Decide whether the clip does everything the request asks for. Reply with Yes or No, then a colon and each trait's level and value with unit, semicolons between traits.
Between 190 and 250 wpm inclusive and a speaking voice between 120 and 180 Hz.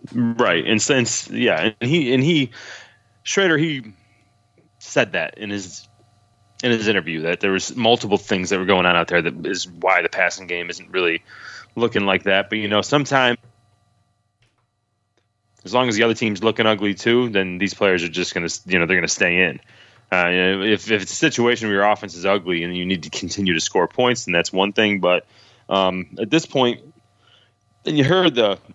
No: fast, 205 wpm; low, 105 Hz